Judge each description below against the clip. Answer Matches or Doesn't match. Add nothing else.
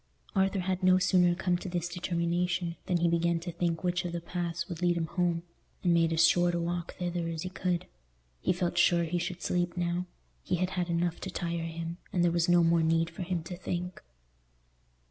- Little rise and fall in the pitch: Matches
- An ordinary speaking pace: Doesn't match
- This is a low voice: Doesn't match